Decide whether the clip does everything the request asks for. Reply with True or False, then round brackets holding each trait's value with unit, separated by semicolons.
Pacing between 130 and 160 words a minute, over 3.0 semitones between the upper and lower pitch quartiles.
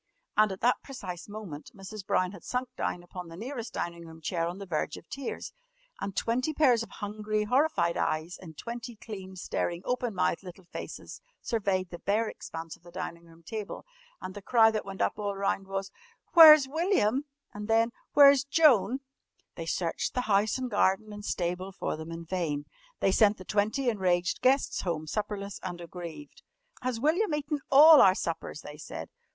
False (185 wpm; 5.4 semitones)